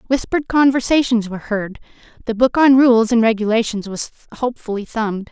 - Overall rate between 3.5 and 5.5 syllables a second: No, 6.0 syllables/s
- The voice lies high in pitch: Yes, high, 235 Hz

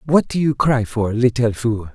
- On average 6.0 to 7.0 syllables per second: No, 4.5 syllables/s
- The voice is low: Yes, low, 120 Hz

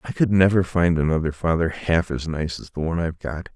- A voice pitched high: No, very low, 85 Hz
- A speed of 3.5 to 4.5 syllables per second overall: No, 6.0 syllables/s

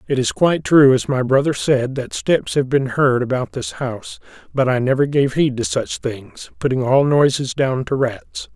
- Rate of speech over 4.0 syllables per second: Yes, 4.7 syllables/s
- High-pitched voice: No, low, 130 Hz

